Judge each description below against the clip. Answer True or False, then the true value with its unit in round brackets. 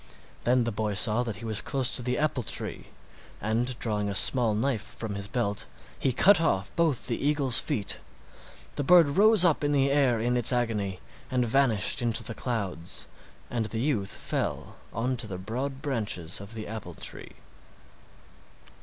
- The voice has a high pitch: False (120 Hz)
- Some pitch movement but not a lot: True (4.1 semitones)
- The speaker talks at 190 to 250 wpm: False (175 wpm)